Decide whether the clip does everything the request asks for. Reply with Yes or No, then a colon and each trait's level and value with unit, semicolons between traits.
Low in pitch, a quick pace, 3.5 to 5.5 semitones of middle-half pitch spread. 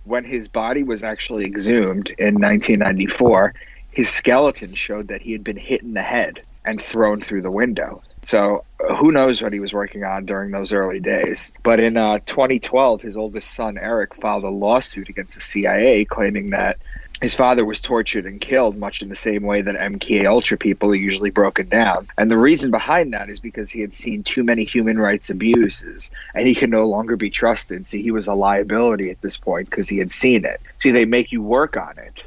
No: low, 110 Hz; fast, 210 wpm; average, 2.7 semitones